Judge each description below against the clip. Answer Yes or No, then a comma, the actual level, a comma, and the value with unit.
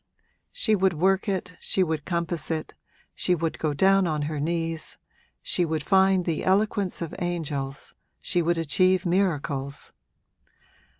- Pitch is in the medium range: Yes, medium, 170 Hz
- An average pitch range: Yes, average, 3.2 semitones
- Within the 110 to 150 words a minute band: Yes, average, 140 wpm